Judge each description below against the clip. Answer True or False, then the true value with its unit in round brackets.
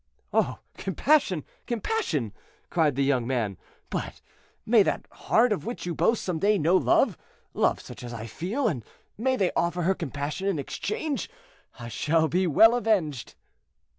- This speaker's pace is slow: False (155 wpm)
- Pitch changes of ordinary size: False (7.7 semitones)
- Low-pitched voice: False (175 Hz)